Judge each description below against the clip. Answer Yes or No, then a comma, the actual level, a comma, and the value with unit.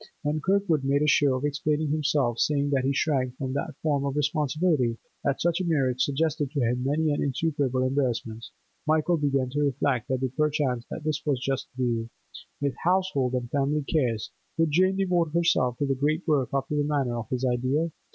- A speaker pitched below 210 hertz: Yes, medium, 140 Hz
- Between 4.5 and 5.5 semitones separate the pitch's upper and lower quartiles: No, average, 3.0 semitones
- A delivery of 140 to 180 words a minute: No, average, 190 wpm